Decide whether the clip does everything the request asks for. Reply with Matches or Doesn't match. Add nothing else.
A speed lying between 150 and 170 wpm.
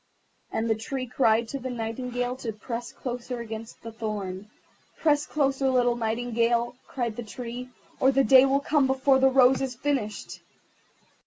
Matches